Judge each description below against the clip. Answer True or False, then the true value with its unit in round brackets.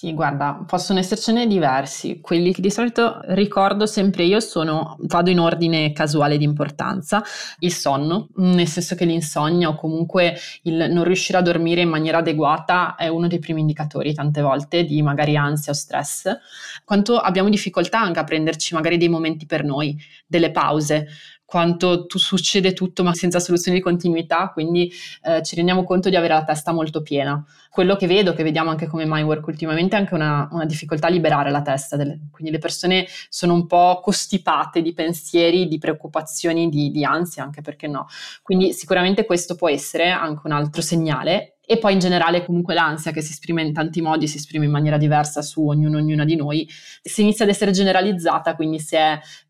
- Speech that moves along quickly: True (190 wpm)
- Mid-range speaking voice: True (165 Hz)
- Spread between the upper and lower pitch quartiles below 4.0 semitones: True (2.6 semitones)